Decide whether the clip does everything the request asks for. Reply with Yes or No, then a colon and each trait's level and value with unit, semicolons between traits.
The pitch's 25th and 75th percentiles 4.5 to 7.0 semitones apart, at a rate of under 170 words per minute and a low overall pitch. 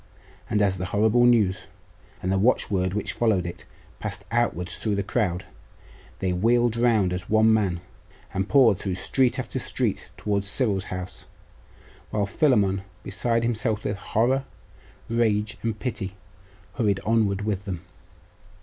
No: average, 3.2 semitones; average, 140 wpm; low, 105 Hz